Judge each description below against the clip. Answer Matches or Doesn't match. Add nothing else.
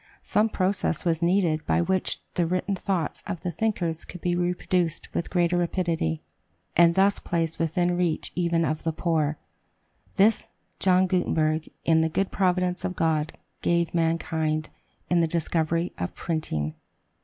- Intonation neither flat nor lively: Doesn't match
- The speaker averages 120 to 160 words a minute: Matches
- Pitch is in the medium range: Matches